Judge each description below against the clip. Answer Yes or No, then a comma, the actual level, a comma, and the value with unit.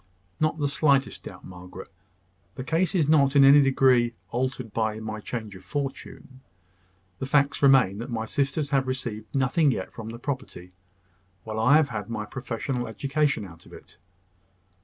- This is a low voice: Yes, low, 130 Hz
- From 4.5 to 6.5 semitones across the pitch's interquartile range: No, average, 4.1 semitones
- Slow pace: No, average, 165 wpm